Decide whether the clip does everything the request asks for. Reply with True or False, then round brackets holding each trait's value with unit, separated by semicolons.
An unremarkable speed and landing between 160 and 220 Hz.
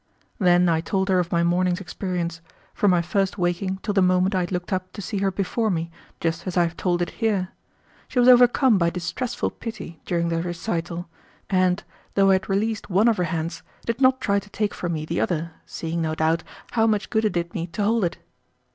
False (225 wpm; 185 Hz)